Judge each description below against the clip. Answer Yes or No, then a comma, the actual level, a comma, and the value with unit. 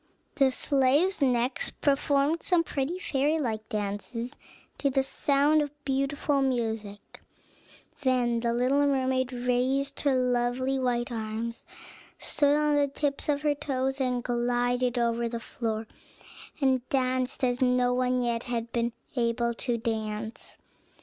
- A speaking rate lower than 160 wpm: Yes, slow, 135 wpm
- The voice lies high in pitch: Yes, very high, 255 Hz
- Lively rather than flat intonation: No, average, 2.7 semitones